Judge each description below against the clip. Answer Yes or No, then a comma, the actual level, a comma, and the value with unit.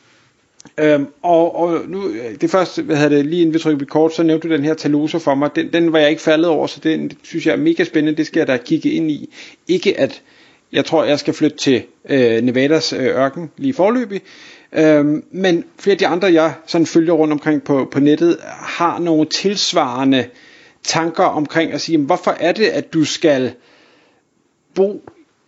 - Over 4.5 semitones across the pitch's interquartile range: No, average, 3.0 semitones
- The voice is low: No, medium, 160 Hz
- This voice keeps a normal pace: Yes, average, 200 wpm